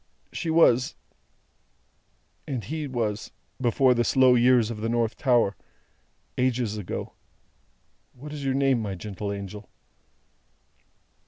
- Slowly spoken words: Yes, slow, 115 wpm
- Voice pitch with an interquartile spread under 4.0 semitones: Yes, average, 3.6 semitones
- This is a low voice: Yes, low, 120 Hz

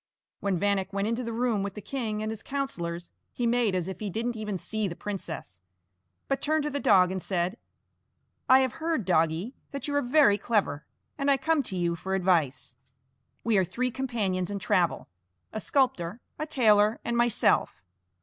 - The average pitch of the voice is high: Yes, high, 210 Hz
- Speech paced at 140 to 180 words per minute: No, average, 190 wpm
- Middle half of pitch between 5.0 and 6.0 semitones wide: Yes, wide, 5.4 semitones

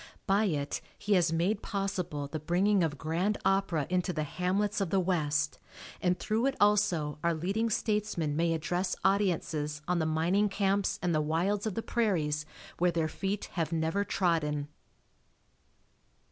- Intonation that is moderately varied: Yes, average, 4.0 semitones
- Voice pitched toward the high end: No, medium, 180 Hz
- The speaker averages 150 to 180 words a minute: Yes, average, 160 wpm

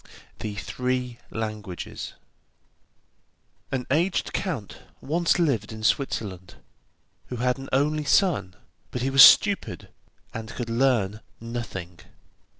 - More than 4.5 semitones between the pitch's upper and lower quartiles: No, average, 4.0 semitones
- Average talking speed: No, slow, 110 wpm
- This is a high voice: No, low, 125 Hz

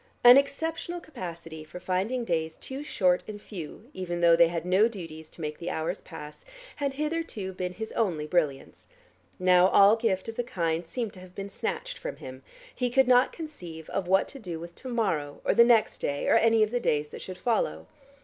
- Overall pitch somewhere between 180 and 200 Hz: Yes, high, 190 Hz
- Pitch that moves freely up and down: Yes, wide, 6.3 semitones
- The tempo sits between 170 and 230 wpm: Yes, fast, 205 wpm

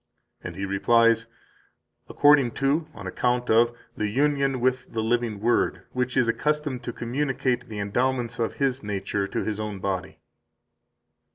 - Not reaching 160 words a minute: Yes, average, 150 wpm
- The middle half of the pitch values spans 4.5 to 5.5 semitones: No, average, 3.4 semitones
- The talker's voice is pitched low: Yes, low, 120 Hz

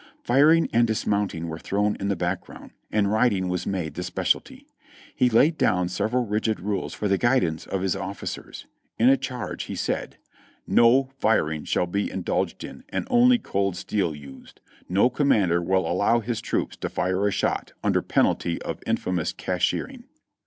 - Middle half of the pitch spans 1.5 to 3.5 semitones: No, average, 4.7 semitones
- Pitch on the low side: Yes, low, 100 Hz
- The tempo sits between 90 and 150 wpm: No, average, 165 wpm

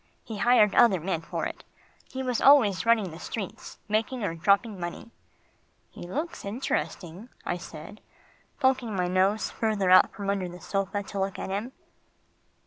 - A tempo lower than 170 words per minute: Yes, average, 160 wpm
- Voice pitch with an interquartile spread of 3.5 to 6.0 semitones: Yes, average, 3.9 semitones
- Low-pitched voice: No, high, 200 Hz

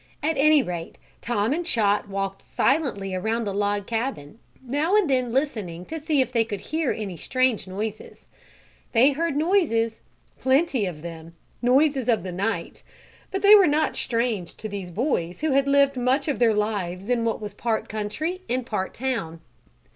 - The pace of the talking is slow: No, average, 175 wpm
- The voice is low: No, high, 230 Hz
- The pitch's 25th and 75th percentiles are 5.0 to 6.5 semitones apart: Yes, wide, 5.6 semitones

